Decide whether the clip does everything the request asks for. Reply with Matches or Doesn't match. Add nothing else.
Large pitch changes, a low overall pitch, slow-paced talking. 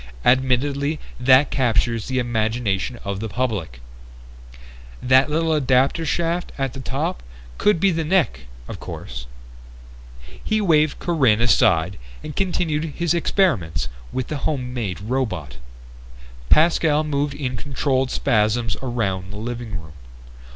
Matches